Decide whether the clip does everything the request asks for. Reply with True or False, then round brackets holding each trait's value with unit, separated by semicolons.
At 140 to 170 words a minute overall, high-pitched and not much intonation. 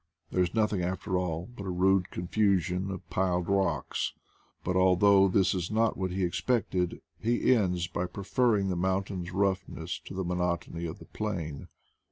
False (165 wpm; 95 Hz; 1.9 semitones)